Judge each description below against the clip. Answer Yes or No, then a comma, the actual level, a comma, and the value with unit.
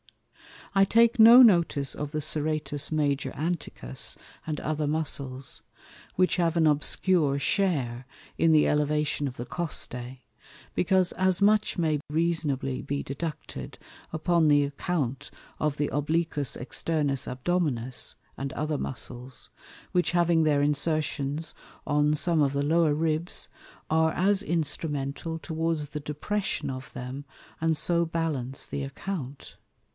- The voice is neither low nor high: Yes, medium, 150 Hz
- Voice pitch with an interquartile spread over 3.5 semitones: No, average, 3.1 semitones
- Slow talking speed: Yes, slow, 130 wpm